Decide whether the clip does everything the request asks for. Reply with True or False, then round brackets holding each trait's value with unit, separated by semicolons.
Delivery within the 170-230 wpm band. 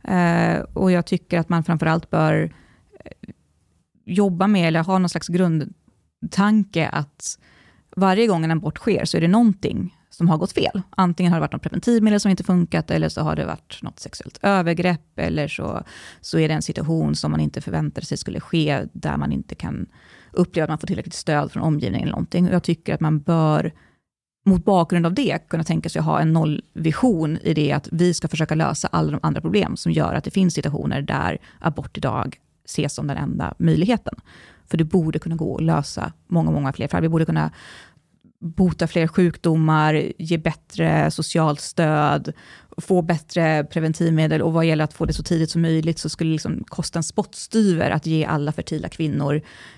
True (195 wpm)